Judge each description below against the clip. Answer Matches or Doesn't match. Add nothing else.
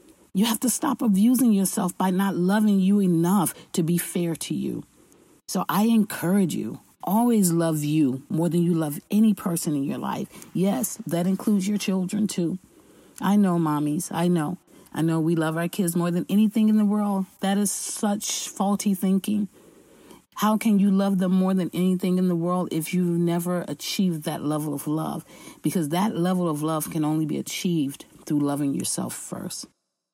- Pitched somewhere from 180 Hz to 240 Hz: Matches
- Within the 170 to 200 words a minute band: Matches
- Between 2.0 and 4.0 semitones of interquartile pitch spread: Matches